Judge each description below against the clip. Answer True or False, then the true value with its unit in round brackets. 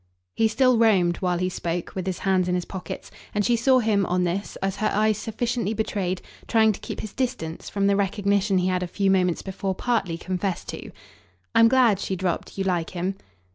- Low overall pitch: False (195 Hz)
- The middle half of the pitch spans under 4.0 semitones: True (3.1 semitones)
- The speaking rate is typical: False (210 wpm)